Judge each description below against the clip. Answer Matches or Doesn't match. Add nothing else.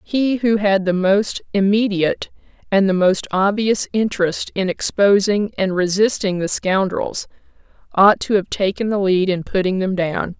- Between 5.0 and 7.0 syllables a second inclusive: Doesn't match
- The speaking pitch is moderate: Doesn't match